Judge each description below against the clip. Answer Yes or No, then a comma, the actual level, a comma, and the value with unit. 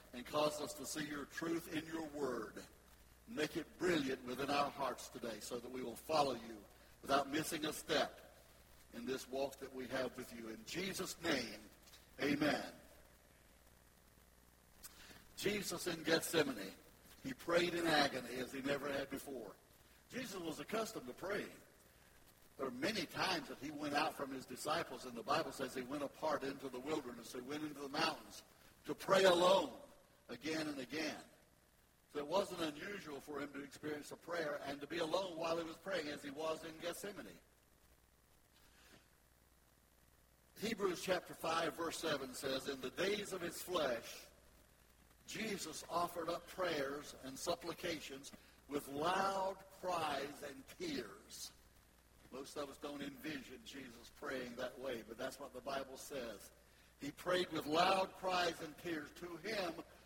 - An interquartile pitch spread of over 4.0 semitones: Yes, average, 5.2 semitones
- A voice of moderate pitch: Yes, medium, 145 Hz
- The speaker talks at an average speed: Yes, average, 160 wpm